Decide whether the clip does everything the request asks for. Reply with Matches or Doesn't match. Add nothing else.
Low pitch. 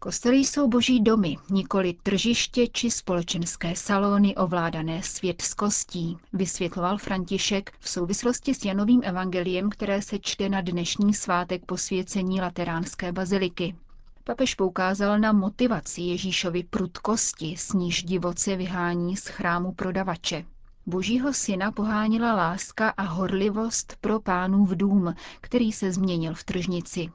Doesn't match